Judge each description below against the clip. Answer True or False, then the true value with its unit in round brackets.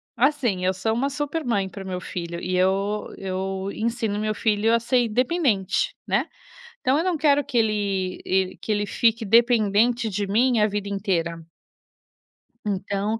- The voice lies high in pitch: True (210 Hz)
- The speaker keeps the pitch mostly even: False (3.8 semitones)